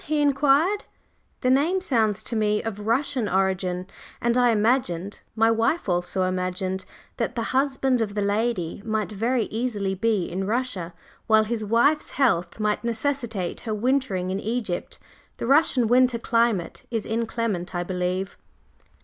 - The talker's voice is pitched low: No, high, 225 Hz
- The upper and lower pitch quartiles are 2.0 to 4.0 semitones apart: No, average, 4.5 semitones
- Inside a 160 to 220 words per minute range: No, average, 150 wpm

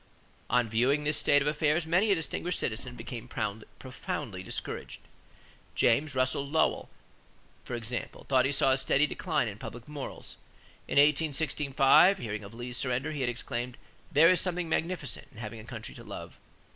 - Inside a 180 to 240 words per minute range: No, average, 165 wpm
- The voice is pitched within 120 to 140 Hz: Yes, low, 135 Hz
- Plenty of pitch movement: No, average, 4.2 semitones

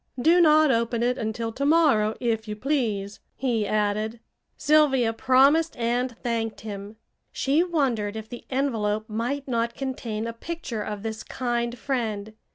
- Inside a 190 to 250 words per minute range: No, average, 150 wpm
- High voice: Yes, high, 235 Hz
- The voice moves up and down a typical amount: Yes, average, 3.7 semitones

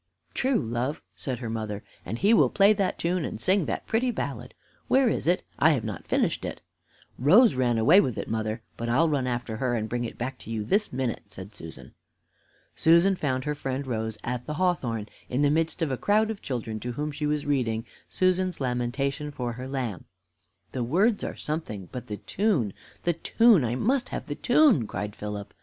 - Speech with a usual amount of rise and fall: No, wide, 7.0 semitones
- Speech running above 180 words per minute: Yes, fast, 205 wpm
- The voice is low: Yes, low, 130 Hz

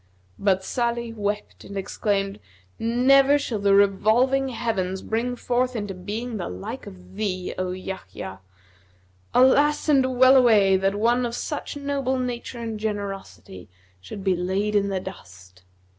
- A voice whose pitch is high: Yes, high, 210 Hz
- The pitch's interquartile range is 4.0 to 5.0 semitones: Yes, average, 4.5 semitones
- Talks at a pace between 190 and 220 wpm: No, average, 145 wpm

